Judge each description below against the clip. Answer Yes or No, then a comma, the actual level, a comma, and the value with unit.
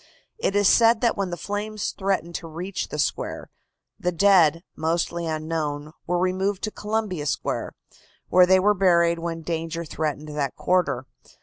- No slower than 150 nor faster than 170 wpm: Yes, average, 160 wpm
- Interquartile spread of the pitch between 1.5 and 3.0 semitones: No, average, 3.4 semitones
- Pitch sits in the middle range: Yes, medium, 175 Hz